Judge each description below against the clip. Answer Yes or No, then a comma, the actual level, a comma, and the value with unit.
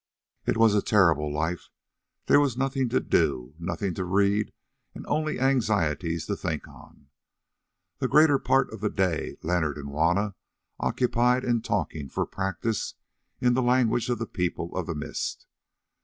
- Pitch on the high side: No, low, 100 Hz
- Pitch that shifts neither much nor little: No, wide, 6.8 semitones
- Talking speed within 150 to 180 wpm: Yes, average, 155 wpm